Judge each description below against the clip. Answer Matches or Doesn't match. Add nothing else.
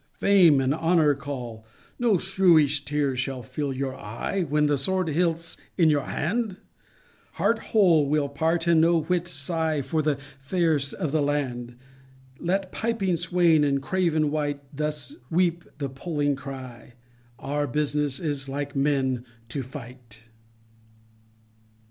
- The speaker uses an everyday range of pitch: Matches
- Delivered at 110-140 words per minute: Matches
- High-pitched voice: Doesn't match